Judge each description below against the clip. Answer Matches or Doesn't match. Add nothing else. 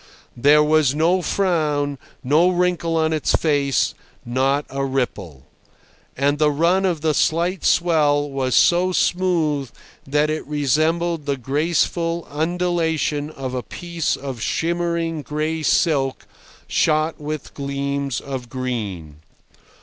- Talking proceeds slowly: Matches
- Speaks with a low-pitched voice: Doesn't match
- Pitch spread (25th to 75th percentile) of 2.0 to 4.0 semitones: Matches